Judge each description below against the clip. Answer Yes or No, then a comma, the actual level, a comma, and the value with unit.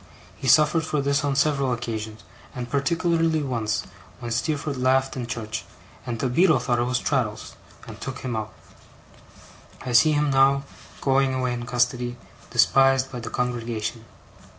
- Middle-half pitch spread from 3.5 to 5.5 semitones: No, average, 2.7 semitones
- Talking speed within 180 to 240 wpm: No, average, 155 wpm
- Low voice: Yes, low, 130 Hz